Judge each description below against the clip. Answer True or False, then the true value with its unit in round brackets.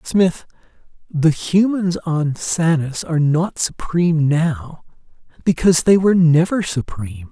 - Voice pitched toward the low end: False (165 Hz)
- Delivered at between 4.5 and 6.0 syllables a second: False (4.2 syllables/s)